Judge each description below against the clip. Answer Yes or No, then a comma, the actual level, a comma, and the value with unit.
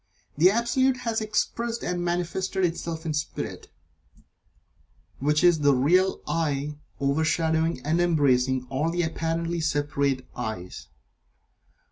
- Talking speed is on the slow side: Yes, slow, 110 wpm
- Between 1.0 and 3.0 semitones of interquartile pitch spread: No, average, 3.5 semitones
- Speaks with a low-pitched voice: No, medium, 160 Hz